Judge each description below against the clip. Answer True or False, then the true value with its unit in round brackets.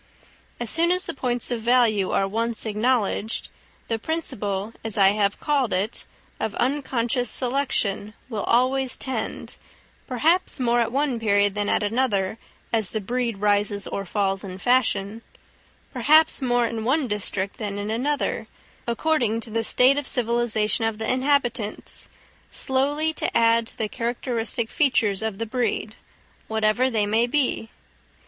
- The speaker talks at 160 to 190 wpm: False (140 wpm)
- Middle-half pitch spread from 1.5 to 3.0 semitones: False (3.4 semitones)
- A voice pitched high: True (230 Hz)